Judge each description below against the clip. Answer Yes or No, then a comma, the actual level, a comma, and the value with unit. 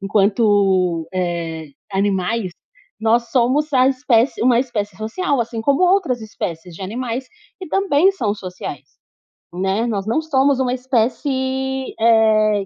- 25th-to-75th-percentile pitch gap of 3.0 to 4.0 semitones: No, average, 4.9 semitones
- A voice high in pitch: Yes, high, 230 Hz